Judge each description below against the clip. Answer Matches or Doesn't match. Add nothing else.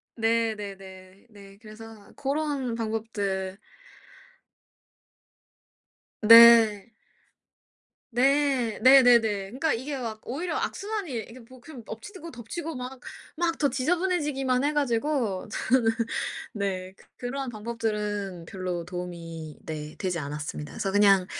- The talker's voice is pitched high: Matches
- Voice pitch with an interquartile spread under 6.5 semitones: Matches